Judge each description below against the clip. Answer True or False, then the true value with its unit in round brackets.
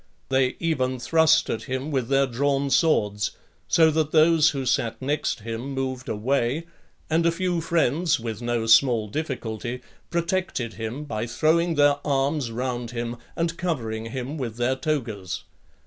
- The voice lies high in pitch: False (135 Hz)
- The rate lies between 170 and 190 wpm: False (155 wpm)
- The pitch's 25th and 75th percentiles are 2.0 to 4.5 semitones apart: False (4.9 semitones)